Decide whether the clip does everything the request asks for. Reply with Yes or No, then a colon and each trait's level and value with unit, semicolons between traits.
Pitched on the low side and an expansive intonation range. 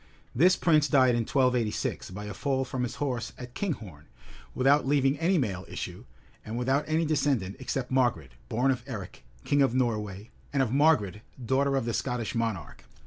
No: low, 125 Hz; average, 3.9 semitones